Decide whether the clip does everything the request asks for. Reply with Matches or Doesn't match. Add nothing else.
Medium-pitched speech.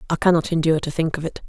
Matches